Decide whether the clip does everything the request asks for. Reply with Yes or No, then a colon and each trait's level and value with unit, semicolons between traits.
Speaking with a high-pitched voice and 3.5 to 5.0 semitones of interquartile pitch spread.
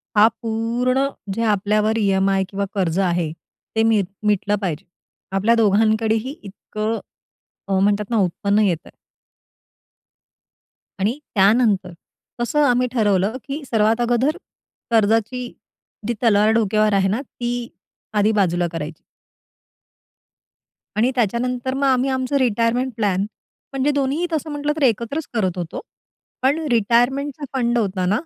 Yes: high, 225 Hz; average, 3.8 semitones